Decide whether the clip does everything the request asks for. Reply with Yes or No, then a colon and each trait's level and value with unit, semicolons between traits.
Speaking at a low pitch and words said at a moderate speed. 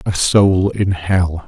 Yes: very low, 95 Hz; average, 160 wpm